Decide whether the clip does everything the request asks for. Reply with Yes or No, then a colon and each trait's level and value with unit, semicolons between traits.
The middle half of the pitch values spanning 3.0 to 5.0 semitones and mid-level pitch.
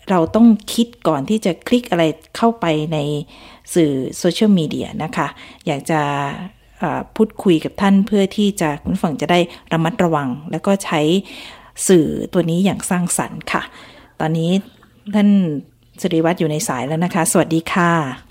Yes: average, 4.0 semitones; medium, 175 Hz